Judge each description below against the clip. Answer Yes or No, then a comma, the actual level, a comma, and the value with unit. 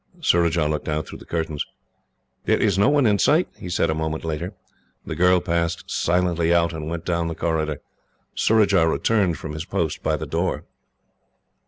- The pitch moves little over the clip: Yes, narrow, 2.3 semitones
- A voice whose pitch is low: Yes, very low, 85 Hz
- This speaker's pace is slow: No, average, 180 wpm